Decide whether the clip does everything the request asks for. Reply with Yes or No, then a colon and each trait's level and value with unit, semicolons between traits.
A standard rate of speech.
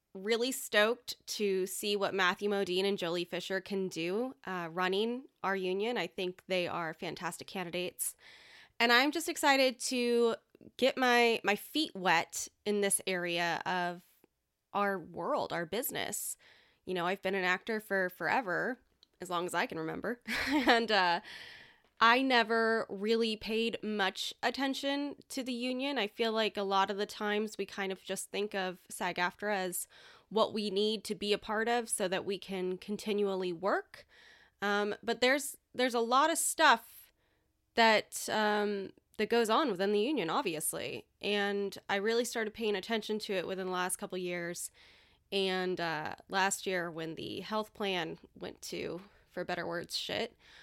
Yes: average, 165 wpm